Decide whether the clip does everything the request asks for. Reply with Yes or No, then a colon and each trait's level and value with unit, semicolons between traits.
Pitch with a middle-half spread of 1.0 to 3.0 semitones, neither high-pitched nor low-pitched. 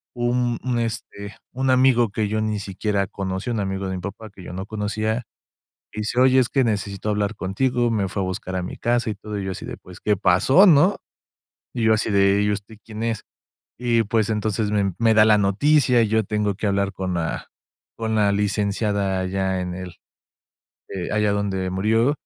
No: average, 2.7 semitones; low, 105 Hz